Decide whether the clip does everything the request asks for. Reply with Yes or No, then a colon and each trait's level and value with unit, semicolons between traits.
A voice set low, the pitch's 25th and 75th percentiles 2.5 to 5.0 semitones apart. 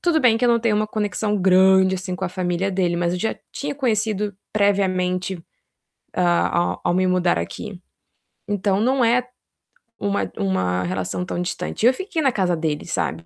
No: high, 190 Hz; average, 3.4 semitones